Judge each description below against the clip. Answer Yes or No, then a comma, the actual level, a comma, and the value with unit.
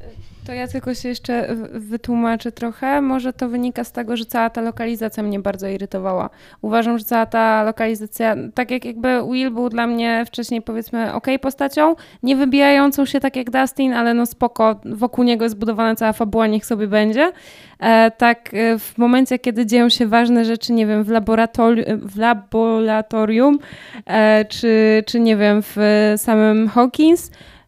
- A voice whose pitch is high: Yes, high, 230 Hz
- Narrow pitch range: Yes, narrow, 1.9 semitones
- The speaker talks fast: Yes, fast, 165 wpm